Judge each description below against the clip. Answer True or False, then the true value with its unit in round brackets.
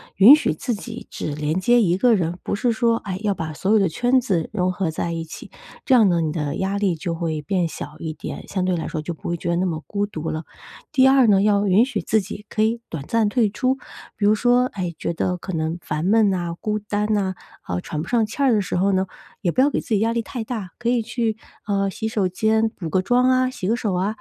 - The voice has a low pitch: False (200 Hz)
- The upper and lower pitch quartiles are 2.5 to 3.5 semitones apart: False (4.7 semitones)